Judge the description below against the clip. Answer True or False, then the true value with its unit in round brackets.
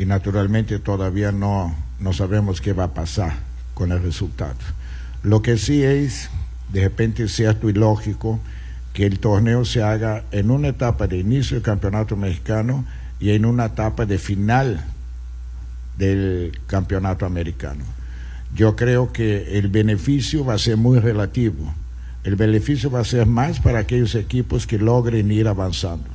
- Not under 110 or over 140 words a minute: False (155 wpm)